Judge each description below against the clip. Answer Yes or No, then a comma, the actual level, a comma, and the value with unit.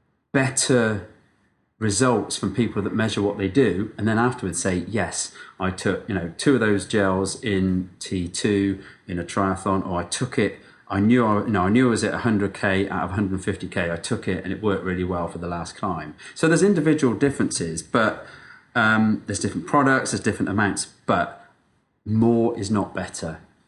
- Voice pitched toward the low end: Yes, low, 100 Hz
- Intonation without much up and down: No, average, 3.6 semitones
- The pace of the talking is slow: No, fast, 205 wpm